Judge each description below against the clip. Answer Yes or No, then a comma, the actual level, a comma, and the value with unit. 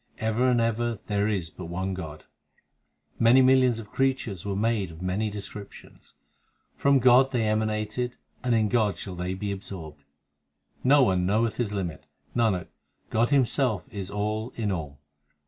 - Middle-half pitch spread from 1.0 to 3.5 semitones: No, average, 3.9 semitones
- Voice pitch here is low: Yes, low, 105 Hz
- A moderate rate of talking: Yes, average, 160 wpm